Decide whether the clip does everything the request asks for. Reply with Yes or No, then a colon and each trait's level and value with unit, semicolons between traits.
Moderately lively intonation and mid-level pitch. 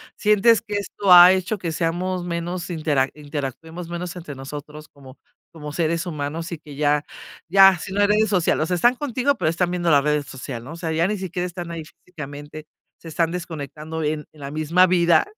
Yes: average, 3.2 semitones; medium, 165 Hz